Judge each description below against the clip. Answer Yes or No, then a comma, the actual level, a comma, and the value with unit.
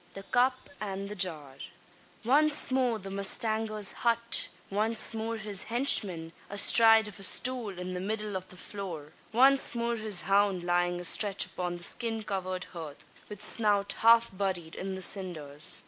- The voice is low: No, high, 200 Hz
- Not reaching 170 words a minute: Yes, average, 160 wpm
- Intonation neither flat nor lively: Yes, average, 3.7 semitones